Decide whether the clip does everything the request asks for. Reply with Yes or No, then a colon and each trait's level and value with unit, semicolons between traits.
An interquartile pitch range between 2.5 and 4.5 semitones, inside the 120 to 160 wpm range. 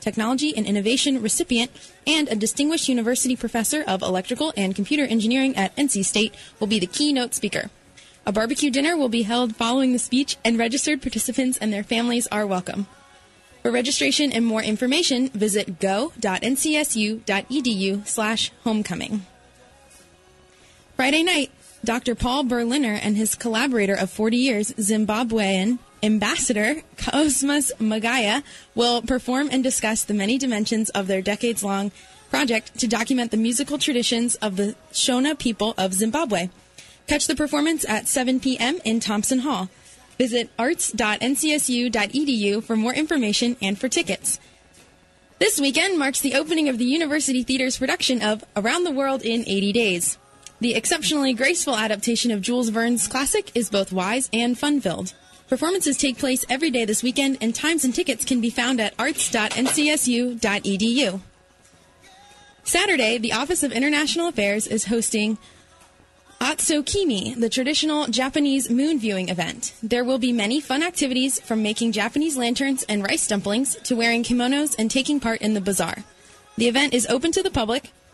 Yes: average, 4.1 semitones; average, 150 wpm